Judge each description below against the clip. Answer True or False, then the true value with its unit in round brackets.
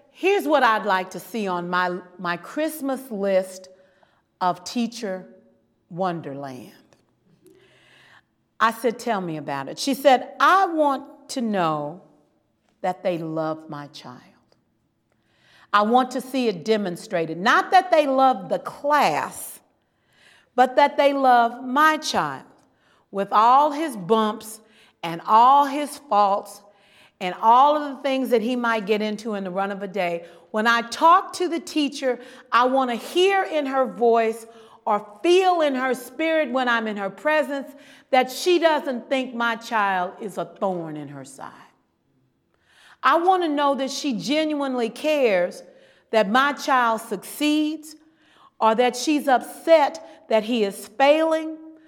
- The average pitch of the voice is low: False (240 Hz)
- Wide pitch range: True (6.6 semitones)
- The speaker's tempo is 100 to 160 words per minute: True (150 wpm)